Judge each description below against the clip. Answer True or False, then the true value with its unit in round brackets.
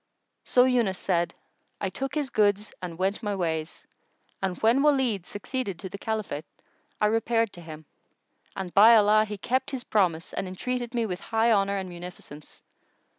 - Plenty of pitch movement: False (4.2 semitones)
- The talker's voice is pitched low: False (205 Hz)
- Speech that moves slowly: False (170 wpm)